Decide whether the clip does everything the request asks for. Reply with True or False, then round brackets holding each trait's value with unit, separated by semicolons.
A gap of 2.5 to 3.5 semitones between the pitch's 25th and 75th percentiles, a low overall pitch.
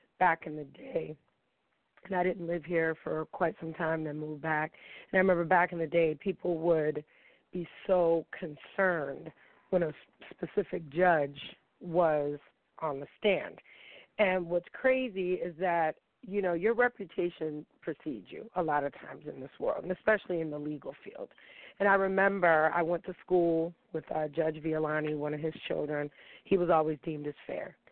False (2.9 semitones; 170 Hz)